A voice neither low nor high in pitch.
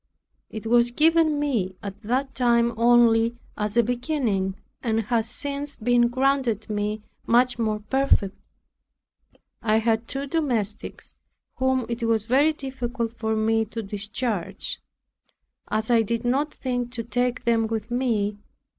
No: high, 235 Hz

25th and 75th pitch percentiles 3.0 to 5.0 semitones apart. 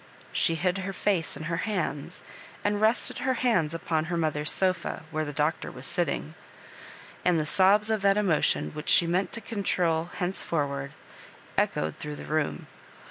Yes: average, 4.2 semitones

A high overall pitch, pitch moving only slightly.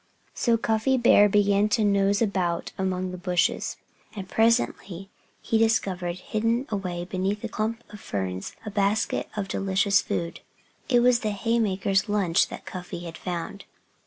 No: high, 200 Hz; average, 3.1 semitones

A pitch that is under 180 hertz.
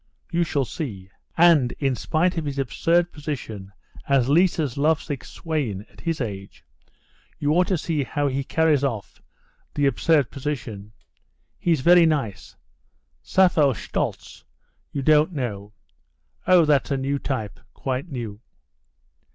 Yes: medium, 140 Hz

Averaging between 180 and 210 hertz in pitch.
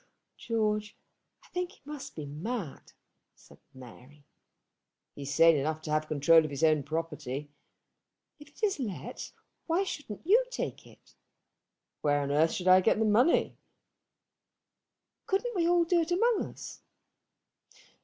Yes: medium, 185 Hz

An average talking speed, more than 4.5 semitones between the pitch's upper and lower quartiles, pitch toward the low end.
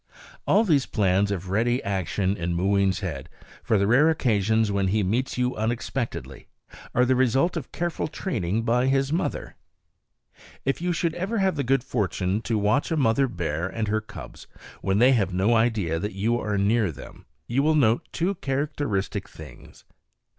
Yes: average, 175 wpm; wide, 5.5 semitones; low, 115 Hz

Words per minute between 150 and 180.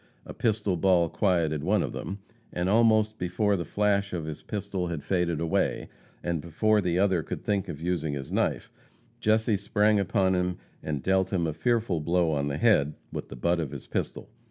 No: average, 195 wpm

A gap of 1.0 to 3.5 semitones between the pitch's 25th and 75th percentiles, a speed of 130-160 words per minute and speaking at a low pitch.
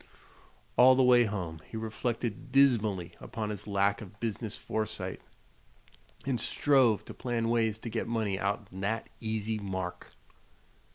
Yes: average, 2.7 semitones; slow, 135 wpm; low, 110 Hz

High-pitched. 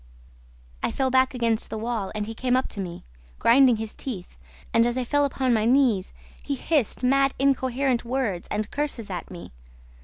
Yes: high, 245 Hz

